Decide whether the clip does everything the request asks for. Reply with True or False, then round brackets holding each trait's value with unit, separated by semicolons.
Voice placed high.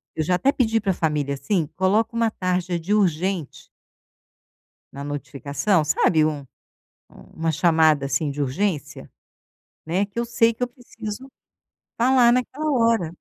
False (180 Hz)